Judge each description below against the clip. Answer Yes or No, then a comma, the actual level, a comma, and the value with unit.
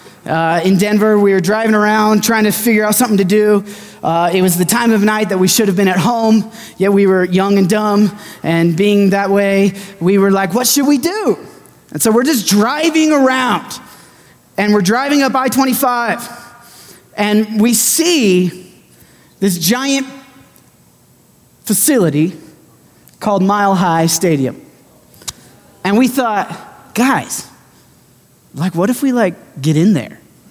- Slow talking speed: No, average, 155 wpm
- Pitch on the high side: Yes, high, 210 Hz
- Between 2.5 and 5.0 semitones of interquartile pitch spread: Yes, average, 3.8 semitones